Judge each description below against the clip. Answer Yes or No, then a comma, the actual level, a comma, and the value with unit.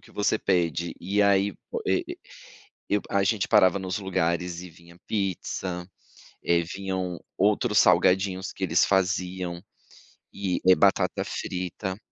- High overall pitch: No, very low, 95 Hz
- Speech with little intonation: Yes, narrow, 1.9 semitones